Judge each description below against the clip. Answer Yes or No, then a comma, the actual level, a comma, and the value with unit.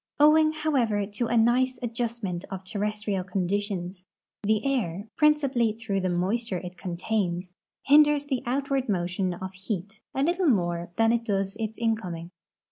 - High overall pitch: Yes, high, 215 Hz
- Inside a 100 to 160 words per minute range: Yes, average, 145 wpm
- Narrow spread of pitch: No, average, 4.9 semitones